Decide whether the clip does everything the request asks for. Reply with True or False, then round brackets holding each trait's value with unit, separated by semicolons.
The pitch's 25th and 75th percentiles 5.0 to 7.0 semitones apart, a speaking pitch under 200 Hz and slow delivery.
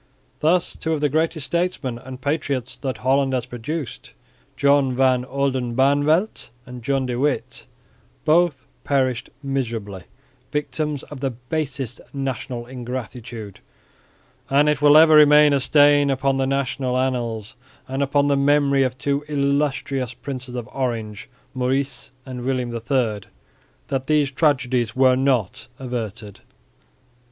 False (2.4 semitones; 135 Hz; 130 wpm)